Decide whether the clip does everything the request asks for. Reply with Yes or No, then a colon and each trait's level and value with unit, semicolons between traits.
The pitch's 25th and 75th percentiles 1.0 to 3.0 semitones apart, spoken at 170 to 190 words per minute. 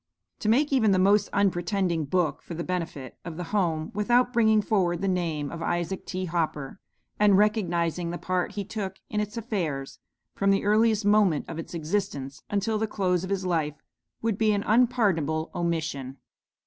No: average, 4.0 semitones; average, 175 wpm